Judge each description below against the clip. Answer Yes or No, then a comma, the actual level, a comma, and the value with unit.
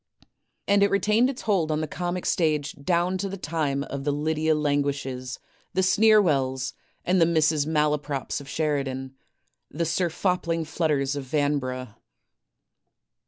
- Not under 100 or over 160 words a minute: Yes, slow, 135 wpm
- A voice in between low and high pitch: Yes, medium, 155 Hz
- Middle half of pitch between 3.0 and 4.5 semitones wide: Yes, average, 3.8 semitones